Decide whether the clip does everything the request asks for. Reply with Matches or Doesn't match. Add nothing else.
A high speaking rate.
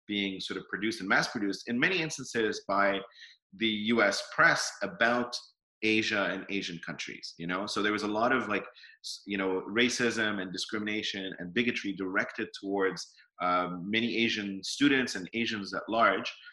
Doesn't match